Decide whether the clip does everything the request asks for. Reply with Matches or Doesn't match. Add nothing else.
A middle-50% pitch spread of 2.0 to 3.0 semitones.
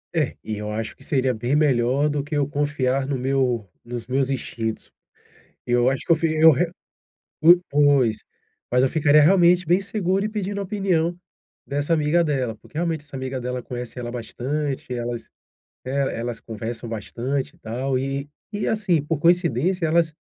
Doesn't match